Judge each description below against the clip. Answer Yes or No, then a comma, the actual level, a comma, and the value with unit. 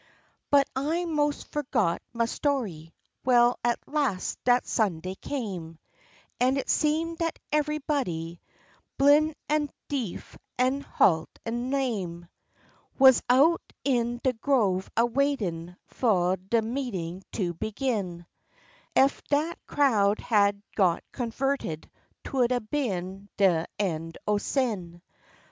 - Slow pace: Yes, slow, 115 wpm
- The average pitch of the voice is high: Yes, high, 240 Hz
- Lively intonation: Yes, wide, 6.9 semitones